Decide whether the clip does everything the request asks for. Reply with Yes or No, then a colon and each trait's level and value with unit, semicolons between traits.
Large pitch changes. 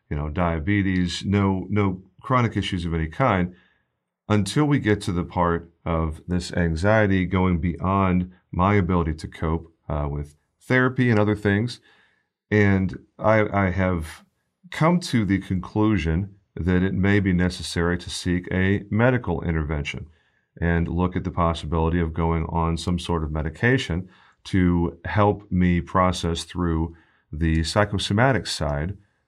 No: average, 3.4 semitones